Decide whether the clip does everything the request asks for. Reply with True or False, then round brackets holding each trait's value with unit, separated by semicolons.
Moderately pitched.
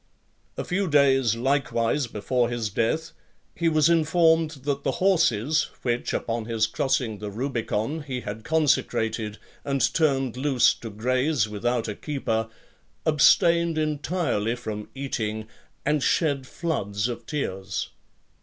False (130 Hz)